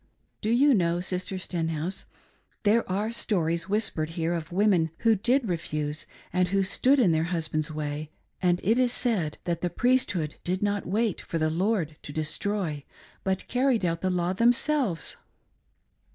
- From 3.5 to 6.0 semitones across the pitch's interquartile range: Yes, average, 4.7 semitones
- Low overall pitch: No, medium, 180 Hz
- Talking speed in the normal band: Yes, average, 165 wpm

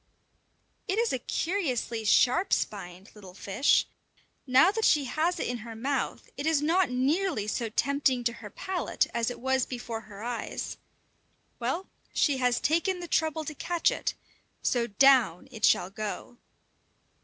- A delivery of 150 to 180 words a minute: Yes, average, 155 wpm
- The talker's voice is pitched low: No, very high, 255 Hz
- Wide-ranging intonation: Yes, wide, 5.8 semitones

